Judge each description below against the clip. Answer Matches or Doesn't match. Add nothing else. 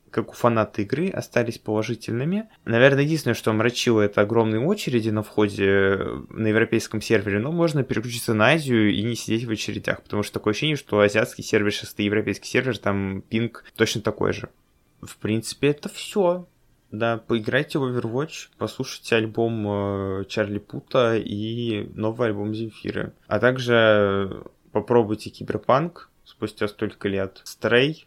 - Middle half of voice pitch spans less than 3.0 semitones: Matches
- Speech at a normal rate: Matches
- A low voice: Matches